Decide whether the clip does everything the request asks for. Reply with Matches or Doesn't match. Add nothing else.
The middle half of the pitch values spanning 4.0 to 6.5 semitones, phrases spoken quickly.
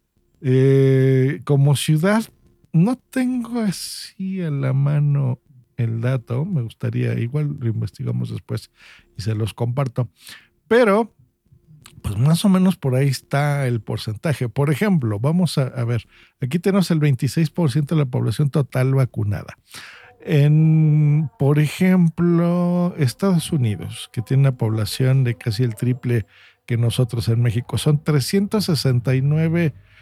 Doesn't match